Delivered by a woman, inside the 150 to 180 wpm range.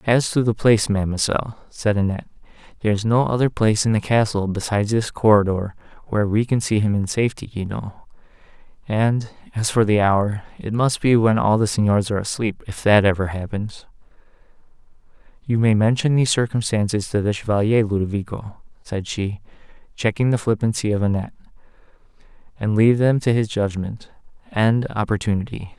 No: male; average, 160 wpm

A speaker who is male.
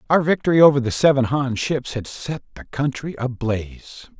Yes: male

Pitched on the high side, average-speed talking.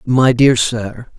No: low, 120 Hz; average, 150 wpm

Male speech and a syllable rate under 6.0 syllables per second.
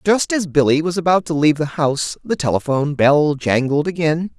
Yes: male; 5.5 syllables/s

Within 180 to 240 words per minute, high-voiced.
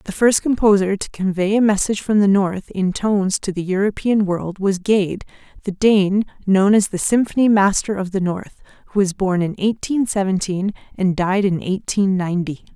Yes: average, 185 wpm; high, 195 Hz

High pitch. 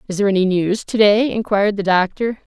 Yes: high, 205 Hz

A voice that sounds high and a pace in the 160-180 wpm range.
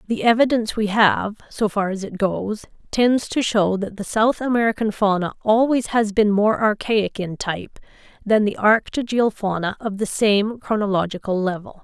Yes: high, 210 Hz; average, 165 wpm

